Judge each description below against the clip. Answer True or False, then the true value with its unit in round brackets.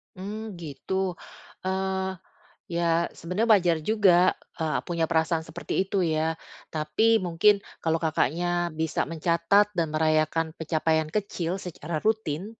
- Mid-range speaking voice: True (170 Hz)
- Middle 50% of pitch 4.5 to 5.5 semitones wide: False (3.0 semitones)